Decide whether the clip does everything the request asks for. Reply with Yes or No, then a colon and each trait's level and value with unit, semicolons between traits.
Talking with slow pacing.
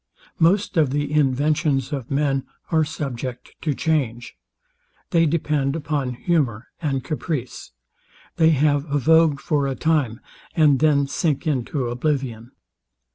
Yes: slow, 130 wpm